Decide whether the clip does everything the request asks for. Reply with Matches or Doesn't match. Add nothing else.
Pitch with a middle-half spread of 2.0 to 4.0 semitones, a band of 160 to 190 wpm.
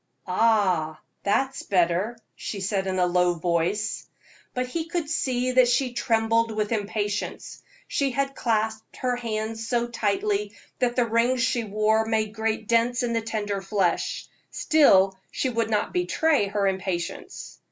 Doesn't match